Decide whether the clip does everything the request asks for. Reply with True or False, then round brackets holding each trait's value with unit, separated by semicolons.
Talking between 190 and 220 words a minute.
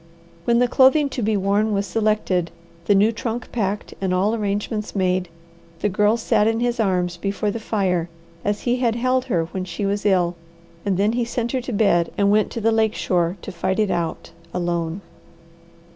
True (195 wpm)